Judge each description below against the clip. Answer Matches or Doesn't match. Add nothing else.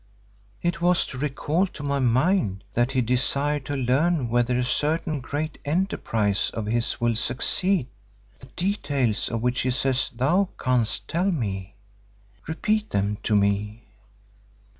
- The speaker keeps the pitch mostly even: Doesn't match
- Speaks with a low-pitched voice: Matches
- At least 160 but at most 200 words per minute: Doesn't match